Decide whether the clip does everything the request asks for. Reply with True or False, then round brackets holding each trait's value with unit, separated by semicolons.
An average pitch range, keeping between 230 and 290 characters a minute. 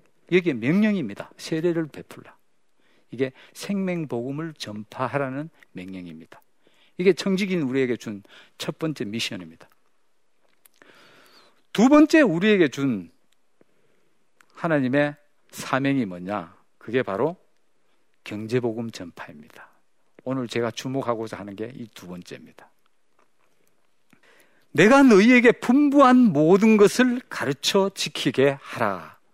False (9.0 semitones; 240 characters per minute)